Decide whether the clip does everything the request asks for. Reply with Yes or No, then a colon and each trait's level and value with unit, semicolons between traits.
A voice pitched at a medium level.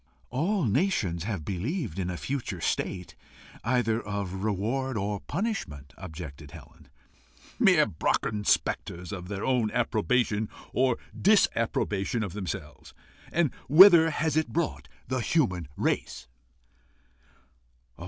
No: low, 105 Hz